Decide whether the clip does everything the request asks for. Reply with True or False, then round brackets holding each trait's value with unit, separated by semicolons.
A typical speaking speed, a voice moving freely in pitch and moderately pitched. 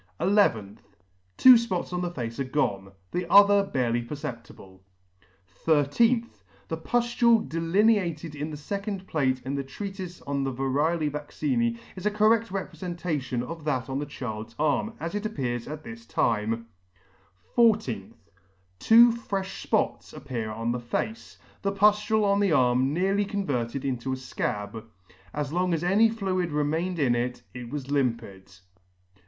True (150 wpm; 7.9 semitones; 155 Hz)